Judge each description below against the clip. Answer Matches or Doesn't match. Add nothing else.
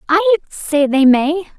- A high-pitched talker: Matches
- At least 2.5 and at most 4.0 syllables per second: Matches